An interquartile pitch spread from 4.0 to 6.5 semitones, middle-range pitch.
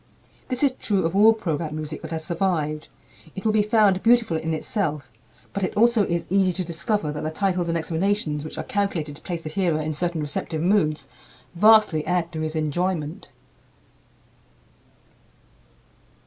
Yes: average, 4.3 semitones; medium, 170 Hz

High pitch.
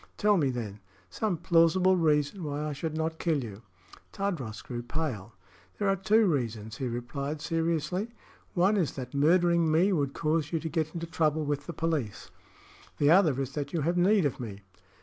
No: medium, 155 Hz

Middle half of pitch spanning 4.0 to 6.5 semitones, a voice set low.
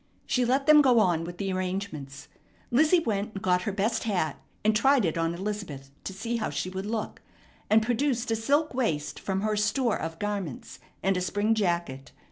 No: average, 4.4 semitones; high, 205 Hz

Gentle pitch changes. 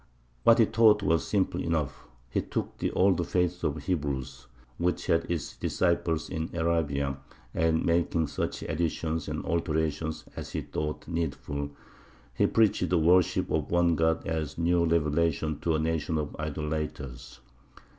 Yes: narrow, 2.1 semitones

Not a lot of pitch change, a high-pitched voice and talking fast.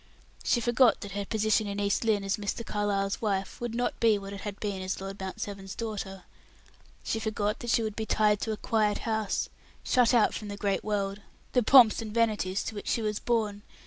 Yes: narrow, 1.9 semitones; high, 210 Hz; fast, 215 wpm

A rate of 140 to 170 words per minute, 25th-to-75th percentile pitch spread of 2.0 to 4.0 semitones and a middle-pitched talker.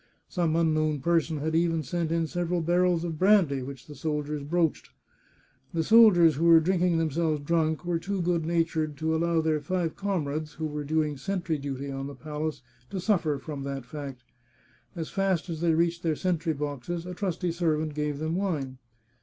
No: average, 180 wpm; narrow, 2.5 semitones; medium, 160 Hz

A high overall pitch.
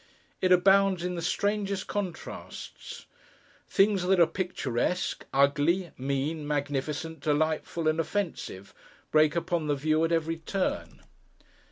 No: medium, 165 Hz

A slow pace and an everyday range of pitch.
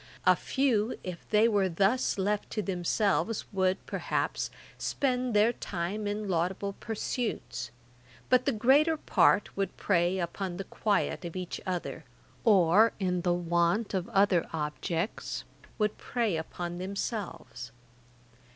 Yes: slow, 130 wpm; average, 3.7 semitones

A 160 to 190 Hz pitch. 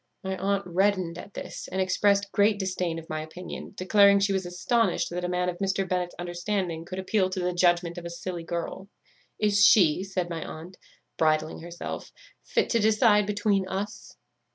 Yes: medium, 185 Hz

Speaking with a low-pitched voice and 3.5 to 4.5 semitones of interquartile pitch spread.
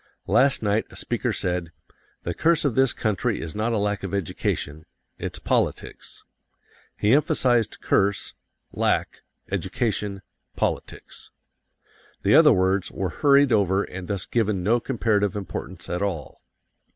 Yes: low, 100 Hz; average, 4.0 semitones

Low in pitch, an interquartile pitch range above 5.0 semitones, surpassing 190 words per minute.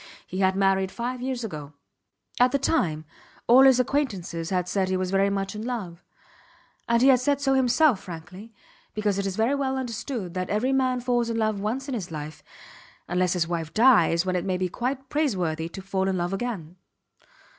No: high, 200 Hz; wide, 5.6 semitones; average, 200 wpm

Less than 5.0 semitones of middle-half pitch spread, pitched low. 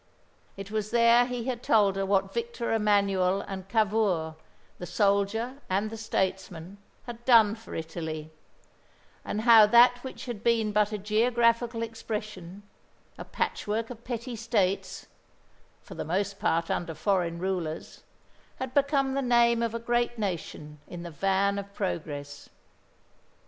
No: average, 3.6 semitones; high, 210 Hz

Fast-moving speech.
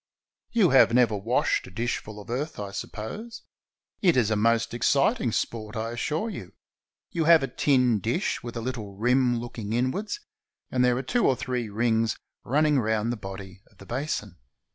No: average, 180 wpm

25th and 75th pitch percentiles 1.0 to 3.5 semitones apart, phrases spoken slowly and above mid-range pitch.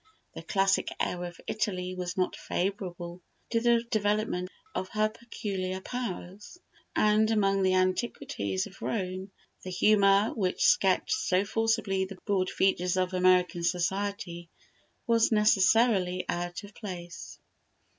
Yes: average, 2.8 semitones; slow, 125 wpm; high, 195 Hz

